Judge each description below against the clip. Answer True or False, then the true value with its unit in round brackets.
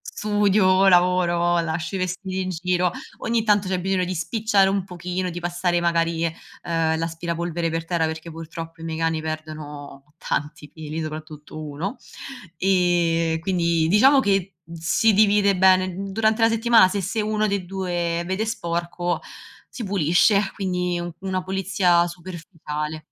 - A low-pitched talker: False (175 Hz)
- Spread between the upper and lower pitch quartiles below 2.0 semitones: False (2.7 semitones)